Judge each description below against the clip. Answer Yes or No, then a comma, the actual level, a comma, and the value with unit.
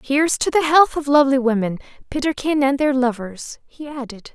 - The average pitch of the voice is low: No, very high, 270 Hz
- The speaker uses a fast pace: No, average, 165 wpm